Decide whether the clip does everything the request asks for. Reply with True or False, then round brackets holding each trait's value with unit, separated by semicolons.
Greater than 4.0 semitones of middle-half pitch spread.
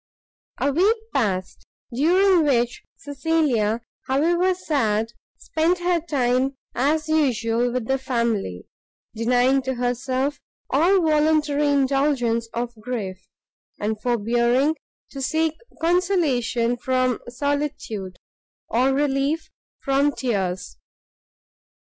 True (4.4 semitones)